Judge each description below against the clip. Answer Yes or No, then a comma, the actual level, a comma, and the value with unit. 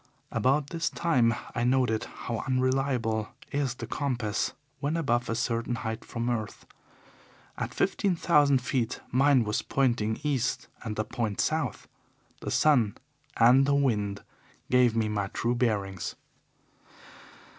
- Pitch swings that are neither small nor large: Yes, average, 3.5 semitones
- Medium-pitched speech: No, low, 120 Hz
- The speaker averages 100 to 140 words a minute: Yes, slow, 135 wpm